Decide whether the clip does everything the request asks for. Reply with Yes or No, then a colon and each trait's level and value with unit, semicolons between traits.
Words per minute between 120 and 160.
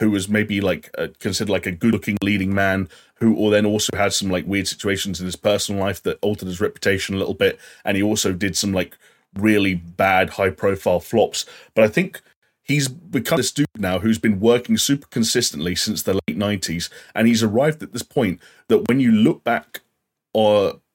No: fast, 205 wpm